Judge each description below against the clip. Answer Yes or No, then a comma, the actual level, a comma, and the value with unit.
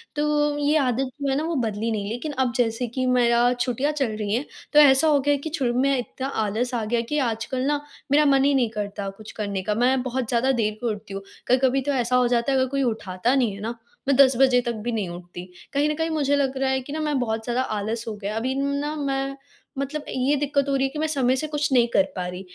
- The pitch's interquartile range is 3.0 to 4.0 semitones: Yes, average, 3.6 semitones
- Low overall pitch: No, very high, 255 Hz